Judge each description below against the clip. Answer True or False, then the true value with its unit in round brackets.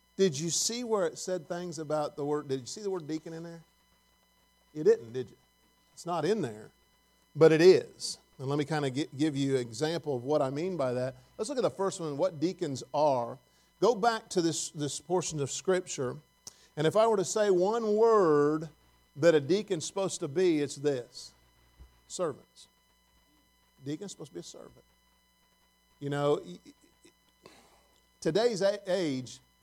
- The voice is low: False (160 Hz)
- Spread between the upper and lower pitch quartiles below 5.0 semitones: True (4.6 semitones)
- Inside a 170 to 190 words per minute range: True (180 wpm)